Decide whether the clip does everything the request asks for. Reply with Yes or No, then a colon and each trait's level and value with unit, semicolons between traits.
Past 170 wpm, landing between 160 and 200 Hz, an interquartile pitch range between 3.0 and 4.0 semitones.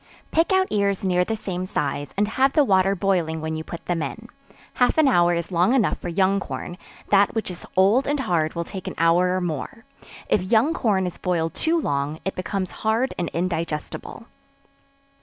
No: average, 195 wpm; medium, 185 Hz; average, 4.4 semitones